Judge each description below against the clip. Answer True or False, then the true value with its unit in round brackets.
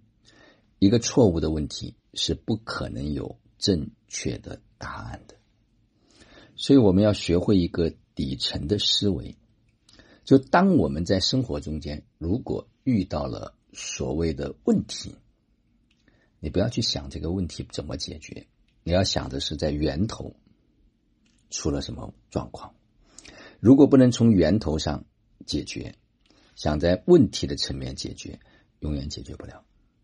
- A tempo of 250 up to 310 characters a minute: False (205 characters per minute)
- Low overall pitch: True (90 Hz)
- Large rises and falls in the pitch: True (6.1 semitones)